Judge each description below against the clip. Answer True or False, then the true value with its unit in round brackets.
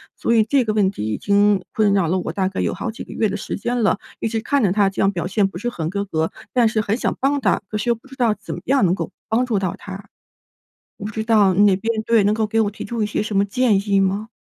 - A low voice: False (210 Hz)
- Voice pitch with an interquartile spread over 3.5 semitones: False (2.5 semitones)